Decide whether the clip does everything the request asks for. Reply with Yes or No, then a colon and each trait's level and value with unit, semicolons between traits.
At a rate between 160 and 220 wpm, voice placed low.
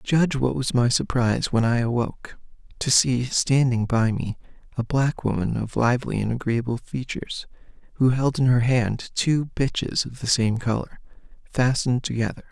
Yes: average, 165 wpm; low, 125 Hz